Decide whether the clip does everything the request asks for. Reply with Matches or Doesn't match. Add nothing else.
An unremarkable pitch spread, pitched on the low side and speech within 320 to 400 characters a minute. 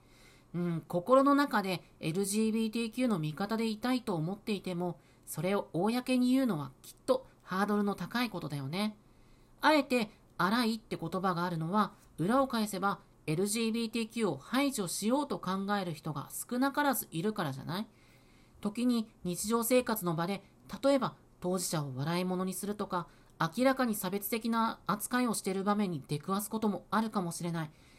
Doesn't match